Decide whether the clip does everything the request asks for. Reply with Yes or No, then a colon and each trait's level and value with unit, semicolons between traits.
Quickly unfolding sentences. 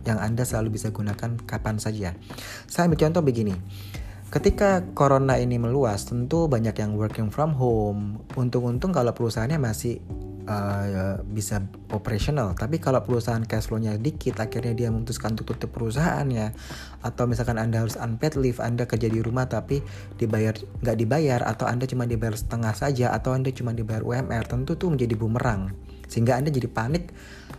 Yes: fast, 160 wpm